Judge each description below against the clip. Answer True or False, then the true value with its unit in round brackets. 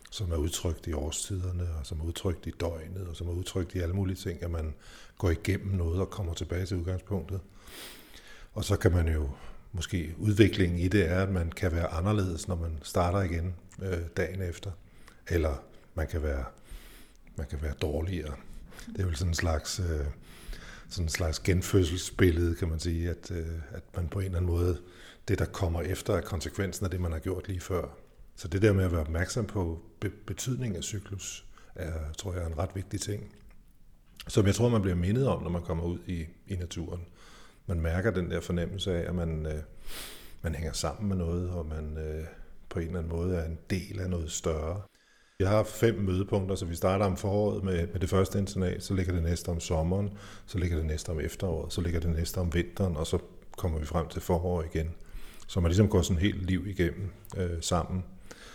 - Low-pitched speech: True (90 Hz)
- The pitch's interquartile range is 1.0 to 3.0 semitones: True (2.6 semitones)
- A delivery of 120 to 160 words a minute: False (210 wpm)